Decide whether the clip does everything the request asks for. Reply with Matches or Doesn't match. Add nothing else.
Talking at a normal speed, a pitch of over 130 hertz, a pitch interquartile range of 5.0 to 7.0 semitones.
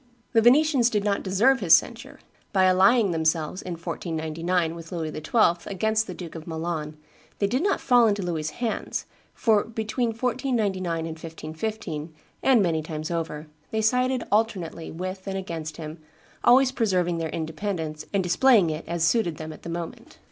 Matches